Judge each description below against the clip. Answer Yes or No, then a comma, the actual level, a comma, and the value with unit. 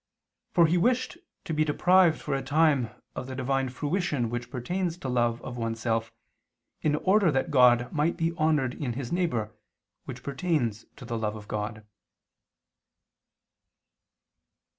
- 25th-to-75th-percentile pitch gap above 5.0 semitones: Yes, wide, 5.4 semitones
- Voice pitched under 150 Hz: Yes, low, 135 Hz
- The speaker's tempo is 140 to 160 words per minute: Yes, average, 150 wpm